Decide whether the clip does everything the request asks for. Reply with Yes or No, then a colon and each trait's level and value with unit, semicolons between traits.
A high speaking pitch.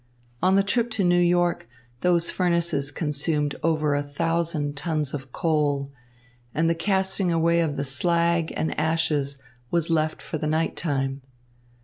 No: medium, 160 Hz